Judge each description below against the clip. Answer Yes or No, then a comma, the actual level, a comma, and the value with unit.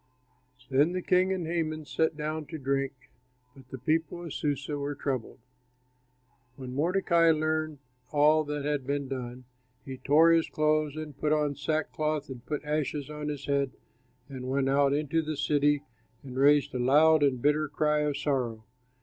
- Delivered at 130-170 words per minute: Yes, average, 165 wpm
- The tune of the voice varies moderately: No, narrow, 2.1 semitones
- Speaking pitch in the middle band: Yes, medium, 150 Hz